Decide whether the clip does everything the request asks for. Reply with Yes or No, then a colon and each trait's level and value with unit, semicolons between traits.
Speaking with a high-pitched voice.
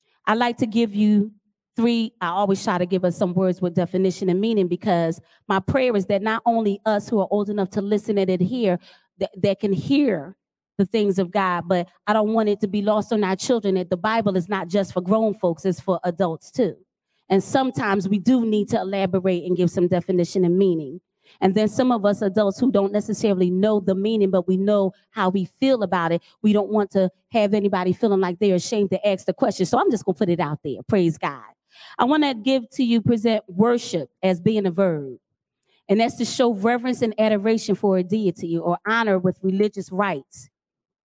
Yes: high, 200 Hz